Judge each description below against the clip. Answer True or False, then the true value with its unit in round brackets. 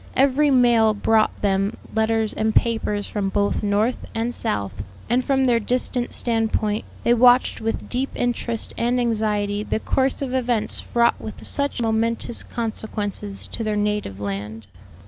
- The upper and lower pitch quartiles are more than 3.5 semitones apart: False (2.7 semitones)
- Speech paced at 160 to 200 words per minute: False (145 wpm)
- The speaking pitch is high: True (225 Hz)